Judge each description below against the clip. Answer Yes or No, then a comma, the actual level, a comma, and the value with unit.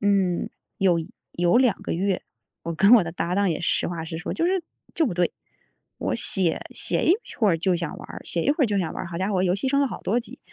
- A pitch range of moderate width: Yes, average, 4.1 semitones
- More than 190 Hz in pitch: No, medium, 185 Hz